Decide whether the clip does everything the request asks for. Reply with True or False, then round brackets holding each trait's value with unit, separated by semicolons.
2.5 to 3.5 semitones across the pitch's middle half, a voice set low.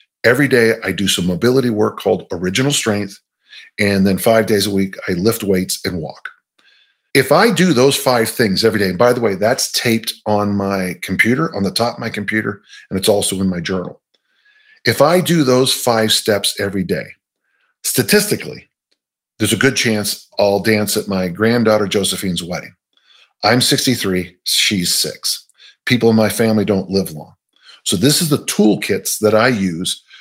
False (4.3 semitones; 110 Hz)